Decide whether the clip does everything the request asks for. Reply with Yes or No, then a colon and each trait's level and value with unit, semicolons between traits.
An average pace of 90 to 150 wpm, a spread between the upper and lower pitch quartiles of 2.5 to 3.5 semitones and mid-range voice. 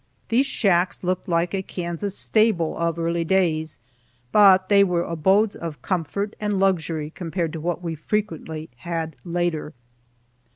Yes: average, 140 wpm; average, 2.9 semitones; medium, 175 Hz